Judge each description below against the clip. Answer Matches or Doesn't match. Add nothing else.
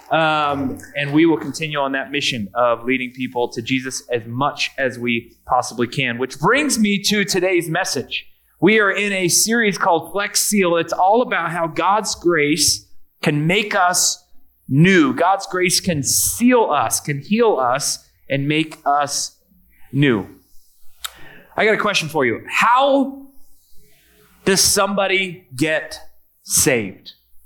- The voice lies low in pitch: Doesn't match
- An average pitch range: Doesn't match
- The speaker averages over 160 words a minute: Doesn't match